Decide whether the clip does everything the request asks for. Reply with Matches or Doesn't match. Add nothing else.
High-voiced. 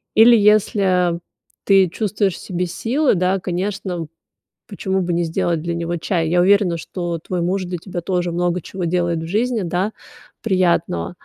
Doesn't match